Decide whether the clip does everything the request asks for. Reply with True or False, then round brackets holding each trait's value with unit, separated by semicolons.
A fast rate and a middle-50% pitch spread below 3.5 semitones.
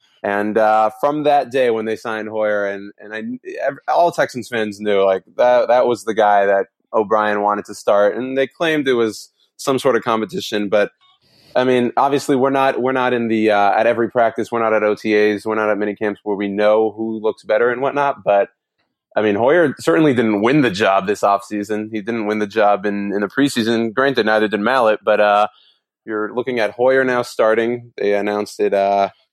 True (210 wpm; 2.9 semitones)